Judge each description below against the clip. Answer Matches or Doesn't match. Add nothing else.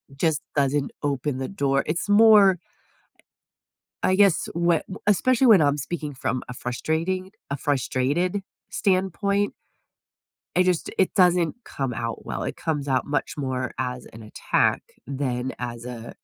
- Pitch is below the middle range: Doesn't match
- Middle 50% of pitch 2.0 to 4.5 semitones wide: Doesn't match